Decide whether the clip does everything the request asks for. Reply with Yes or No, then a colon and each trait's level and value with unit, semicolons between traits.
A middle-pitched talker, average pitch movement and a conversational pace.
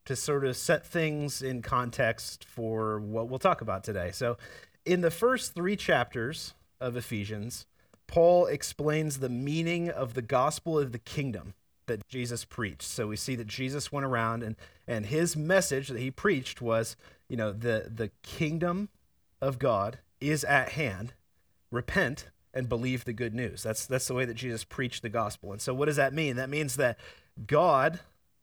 No: low, 125 Hz; average, 4.6 semitones; average, 175 wpm